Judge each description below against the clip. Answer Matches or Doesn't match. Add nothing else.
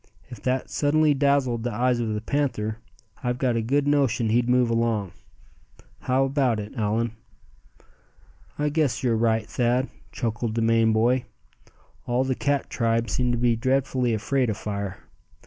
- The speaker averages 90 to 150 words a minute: Doesn't match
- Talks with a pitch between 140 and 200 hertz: Doesn't match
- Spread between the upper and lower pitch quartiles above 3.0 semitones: Doesn't match